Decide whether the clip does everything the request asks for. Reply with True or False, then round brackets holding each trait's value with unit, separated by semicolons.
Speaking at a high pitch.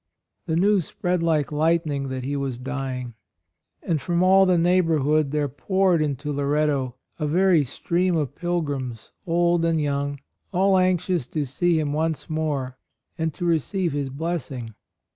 False (155 Hz)